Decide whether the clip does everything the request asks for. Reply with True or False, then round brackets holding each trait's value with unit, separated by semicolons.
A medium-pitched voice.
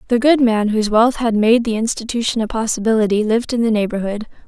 False (225 Hz)